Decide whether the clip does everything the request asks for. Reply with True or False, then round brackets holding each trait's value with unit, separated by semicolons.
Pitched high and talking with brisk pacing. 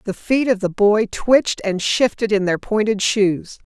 False (210 Hz; 195 wpm)